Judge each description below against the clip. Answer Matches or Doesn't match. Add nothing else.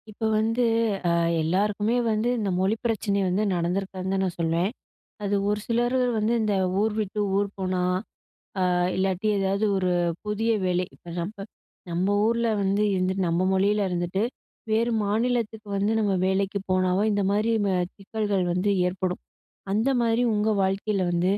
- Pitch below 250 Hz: Matches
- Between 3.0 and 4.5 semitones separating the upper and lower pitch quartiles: Doesn't match